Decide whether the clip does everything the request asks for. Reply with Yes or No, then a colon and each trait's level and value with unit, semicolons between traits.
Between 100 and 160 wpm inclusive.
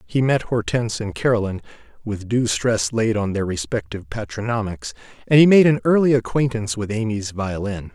Yes: average, 150 wpm